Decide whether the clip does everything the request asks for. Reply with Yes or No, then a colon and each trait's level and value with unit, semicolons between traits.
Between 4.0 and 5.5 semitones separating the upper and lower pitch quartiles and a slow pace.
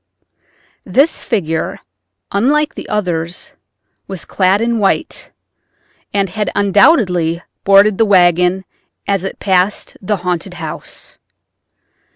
No: average, 2.8 semitones; slow, 105 wpm